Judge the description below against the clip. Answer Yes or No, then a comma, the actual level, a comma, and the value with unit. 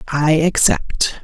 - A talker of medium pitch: Yes, medium, 155 Hz